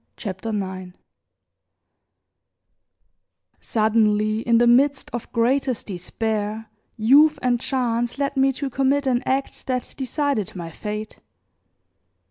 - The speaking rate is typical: No, slow, 105 wpm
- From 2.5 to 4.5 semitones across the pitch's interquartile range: Yes, average, 3.8 semitones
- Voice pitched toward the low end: No, high, 235 Hz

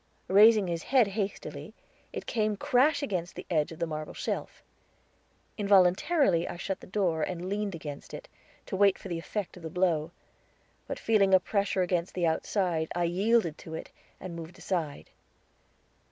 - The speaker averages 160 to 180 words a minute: Yes, average, 170 wpm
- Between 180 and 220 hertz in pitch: Yes, medium, 185 Hz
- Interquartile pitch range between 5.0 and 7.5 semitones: No, average, 3.3 semitones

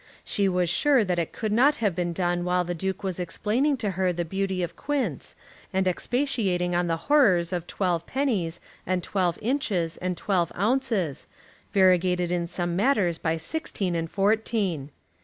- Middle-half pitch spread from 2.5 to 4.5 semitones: Yes, average, 3.4 semitones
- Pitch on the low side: No, medium, 185 Hz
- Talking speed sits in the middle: Yes, average, 170 wpm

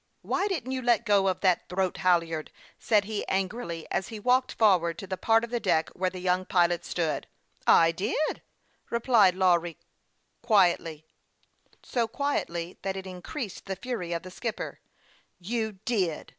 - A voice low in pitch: No, high, 190 Hz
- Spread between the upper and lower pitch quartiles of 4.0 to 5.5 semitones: Yes, average, 4.7 semitones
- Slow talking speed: No, average, 170 wpm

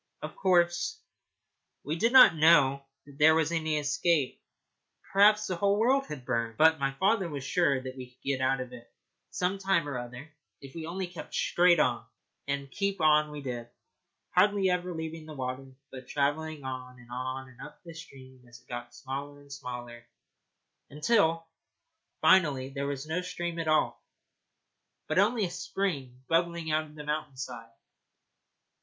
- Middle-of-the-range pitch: Yes, medium, 150 Hz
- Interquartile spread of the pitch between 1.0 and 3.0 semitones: No, average, 4.7 semitones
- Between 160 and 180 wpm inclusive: Yes, average, 170 wpm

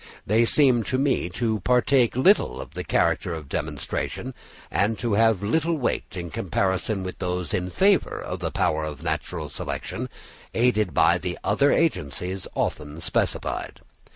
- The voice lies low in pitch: Yes, low, 105 Hz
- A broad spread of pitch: Yes, wide, 6.0 semitones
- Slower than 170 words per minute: Yes, average, 155 wpm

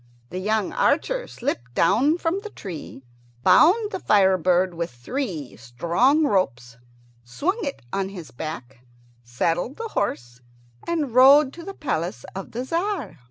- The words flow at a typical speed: Yes, average, 145 wpm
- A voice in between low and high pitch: No, high, 195 Hz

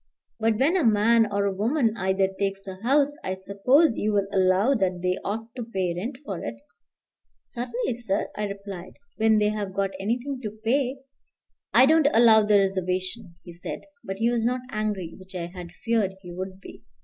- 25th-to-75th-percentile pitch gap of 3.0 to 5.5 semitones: Yes, average, 3.7 semitones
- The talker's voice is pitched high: Yes, high, 205 Hz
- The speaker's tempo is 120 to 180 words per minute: No, average, 190 wpm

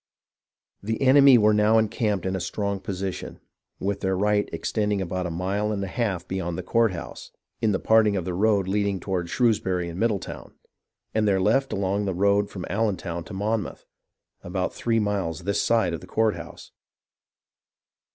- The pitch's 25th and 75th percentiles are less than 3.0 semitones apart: Yes, narrow, 2.5 semitones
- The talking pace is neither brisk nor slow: Yes, average, 170 wpm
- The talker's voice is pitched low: Yes, low, 100 Hz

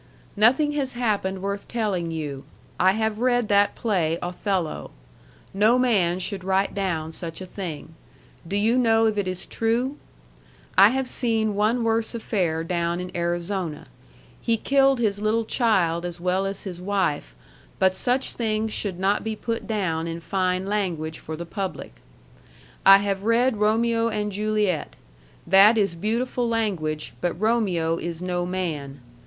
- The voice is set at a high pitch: Yes, high, 200 Hz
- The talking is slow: No, average, 155 wpm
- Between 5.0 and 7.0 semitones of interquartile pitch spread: No, average, 4.1 semitones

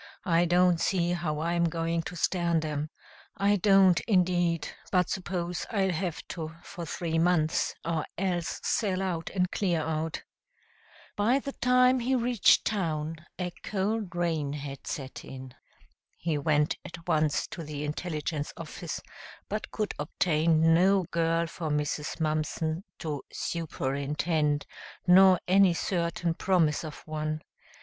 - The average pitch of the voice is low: No, medium, 170 Hz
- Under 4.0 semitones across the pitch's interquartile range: Yes, average, 2.9 semitones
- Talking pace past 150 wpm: No, slow, 135 wpm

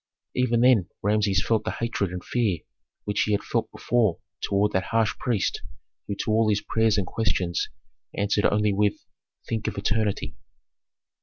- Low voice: Yes, low, 105 Hz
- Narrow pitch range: Yes, narrow, 2.1 semitones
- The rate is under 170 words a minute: Yes, average, 160 wpm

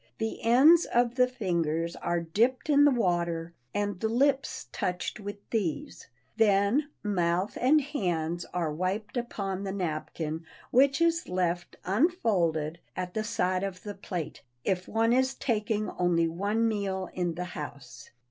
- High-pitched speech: Yes, high, 195 Hz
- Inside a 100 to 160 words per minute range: Yes, average, 145 wpm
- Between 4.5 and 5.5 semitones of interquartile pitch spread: Yes, average, 5.2 semitones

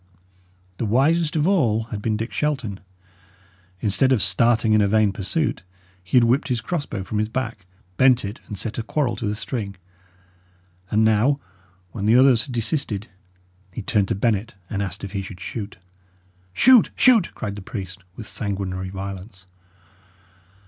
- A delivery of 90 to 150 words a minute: No, average, 165 wpm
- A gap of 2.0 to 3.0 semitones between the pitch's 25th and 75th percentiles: No, average, 4.3 semitones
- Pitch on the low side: Yes, low, 110 Hz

